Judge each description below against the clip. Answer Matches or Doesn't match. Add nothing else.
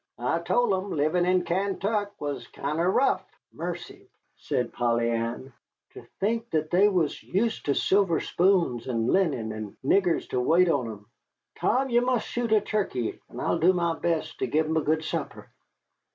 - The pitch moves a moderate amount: Doesn't match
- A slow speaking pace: Doesn't match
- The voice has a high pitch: Doesn't match